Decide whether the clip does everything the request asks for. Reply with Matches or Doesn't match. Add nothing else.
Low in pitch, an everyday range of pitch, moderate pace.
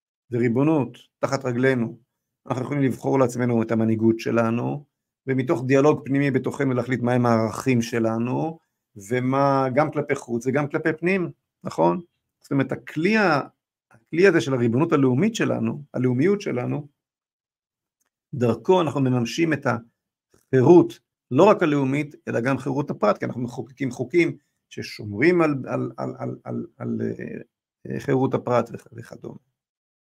Matches